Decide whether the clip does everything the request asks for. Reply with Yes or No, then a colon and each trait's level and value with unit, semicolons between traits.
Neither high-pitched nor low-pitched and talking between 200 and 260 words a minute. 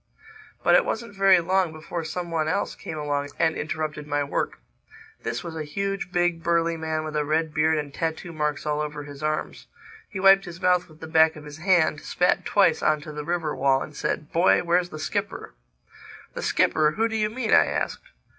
Yes: medium, 160 Hz; fast, 205 wpm